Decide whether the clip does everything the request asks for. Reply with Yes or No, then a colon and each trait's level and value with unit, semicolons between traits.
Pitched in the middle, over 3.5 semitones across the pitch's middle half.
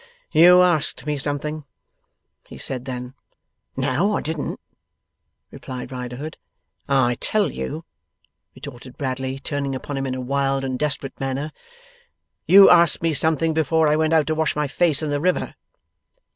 No: medium, 145 Hz; average, 3.2 semitones